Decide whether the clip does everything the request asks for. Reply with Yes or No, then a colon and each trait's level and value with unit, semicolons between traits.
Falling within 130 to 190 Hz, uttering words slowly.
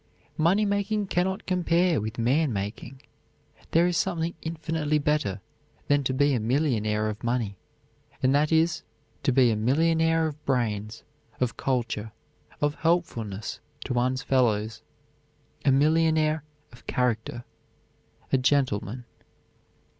Yes: low, 135 Hz; slow, 125 wpm